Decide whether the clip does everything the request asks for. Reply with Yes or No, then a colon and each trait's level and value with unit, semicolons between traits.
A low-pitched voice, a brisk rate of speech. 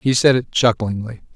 No: low, 115 Hz; average, 175 wpm